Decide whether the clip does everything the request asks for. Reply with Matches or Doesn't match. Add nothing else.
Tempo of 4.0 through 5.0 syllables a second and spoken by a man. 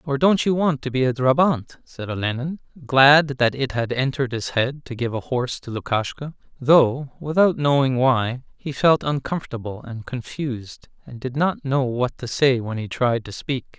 Matches